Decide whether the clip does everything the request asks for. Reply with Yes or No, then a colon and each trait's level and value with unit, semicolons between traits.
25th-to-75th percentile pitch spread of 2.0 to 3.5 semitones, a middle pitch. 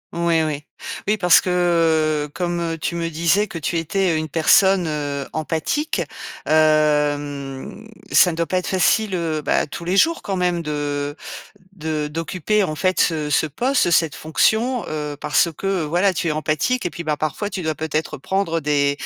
Yes: average, 3.2 semitones; medium, 165 Hz